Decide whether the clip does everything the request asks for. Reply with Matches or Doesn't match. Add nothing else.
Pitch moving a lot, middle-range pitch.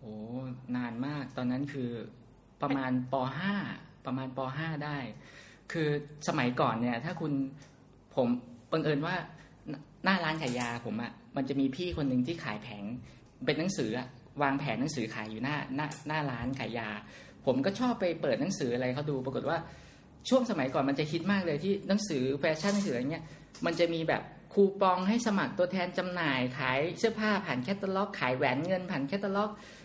Matches